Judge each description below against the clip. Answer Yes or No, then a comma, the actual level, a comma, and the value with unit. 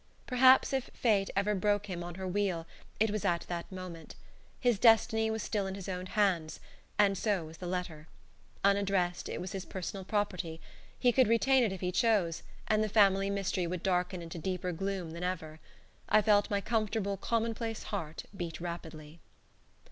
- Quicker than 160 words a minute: Yes, average, 180 wpm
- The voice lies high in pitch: Yes, high, 195 Hz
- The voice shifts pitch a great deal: No, average, 3.2 semitones